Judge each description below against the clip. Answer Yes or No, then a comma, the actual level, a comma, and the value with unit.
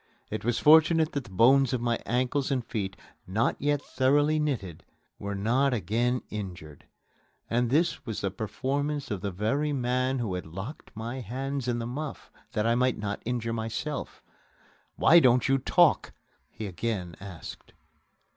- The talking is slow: No, average, 160 wpm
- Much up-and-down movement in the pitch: No, average, 4.6 semitones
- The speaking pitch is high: No, low, 120 Hz